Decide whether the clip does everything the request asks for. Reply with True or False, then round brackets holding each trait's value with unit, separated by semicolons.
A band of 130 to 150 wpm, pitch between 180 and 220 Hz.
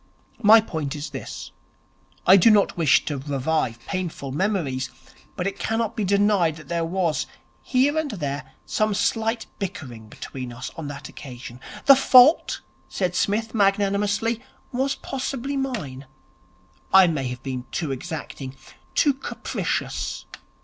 True (135 wpm; 185 Hz)